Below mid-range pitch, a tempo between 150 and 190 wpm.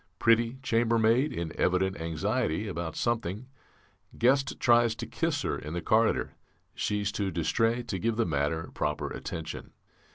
No: low, 105 Hz; average, 140 wpm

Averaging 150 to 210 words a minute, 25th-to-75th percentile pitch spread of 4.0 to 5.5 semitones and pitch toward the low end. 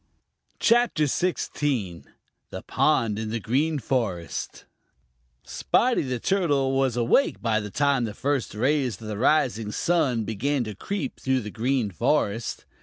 No: average, 140 wpm; average, 4.9 semitones; low, 125 Hz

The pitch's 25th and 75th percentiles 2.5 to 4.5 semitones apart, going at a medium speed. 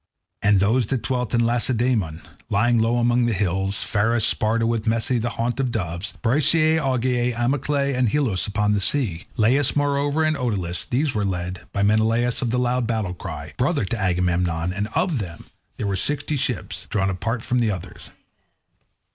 Yes: average, 4.2 semitones; average, 180 wpm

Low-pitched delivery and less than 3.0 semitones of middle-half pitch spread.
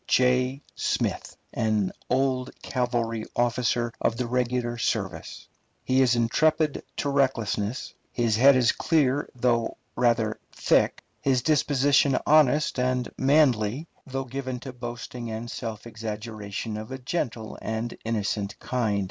Yes: low, 125 Hz; narrow, 2.6 semitones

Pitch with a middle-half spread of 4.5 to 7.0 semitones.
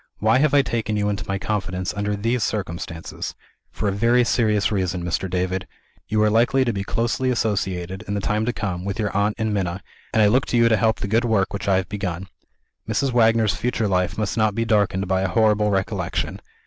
No: average, 2.8 semitones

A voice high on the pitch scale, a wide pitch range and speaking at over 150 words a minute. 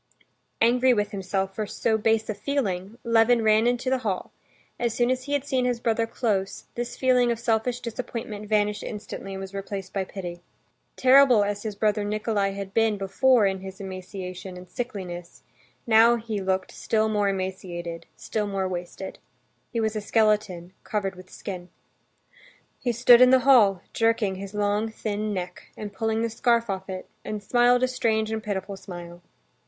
No: high, 210 Hz; average, 3.3 semitones; average, 175 wpm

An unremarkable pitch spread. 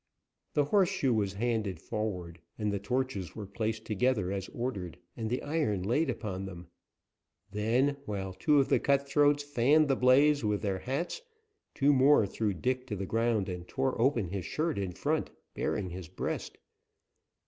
No: wide, 5.7 semitones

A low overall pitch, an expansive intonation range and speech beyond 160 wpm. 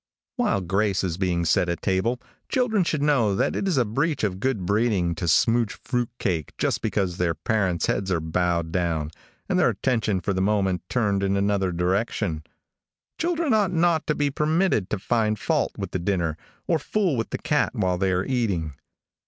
Yes: low, 100 Hz; wide, 6.1 semitones; average, 190 wpm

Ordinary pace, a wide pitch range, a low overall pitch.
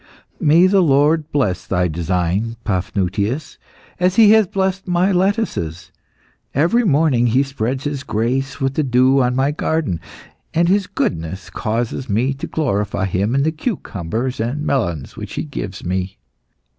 Yes: average, 150 wpm; wide, 8.1 semitones; low, 130 Hz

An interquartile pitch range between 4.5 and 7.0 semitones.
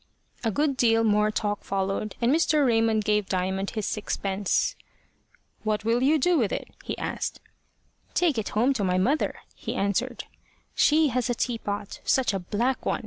No: average, 4.0 semitones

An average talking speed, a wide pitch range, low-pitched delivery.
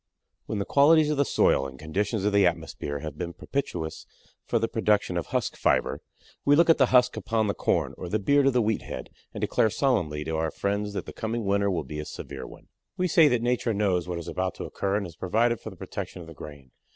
No: fast, 245 wpm; wide, 5.9 semitones; low, 100 Hz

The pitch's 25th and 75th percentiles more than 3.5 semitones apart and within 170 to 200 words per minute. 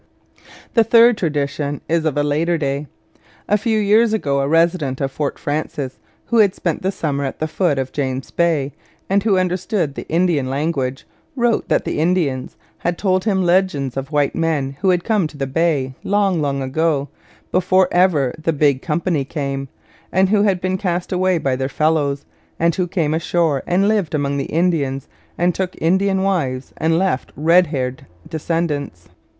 Yes: average, 4.8 semitones; average, 180 wpm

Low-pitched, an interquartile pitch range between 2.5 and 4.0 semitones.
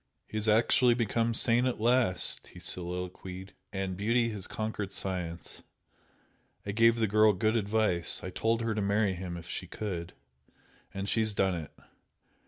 Yes: low, 105 Hz; average, 3.5 semitones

